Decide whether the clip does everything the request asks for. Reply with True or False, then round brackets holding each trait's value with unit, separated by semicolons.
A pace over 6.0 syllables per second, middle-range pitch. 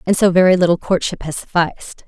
True (6.2 syllables/s; 180 Hz)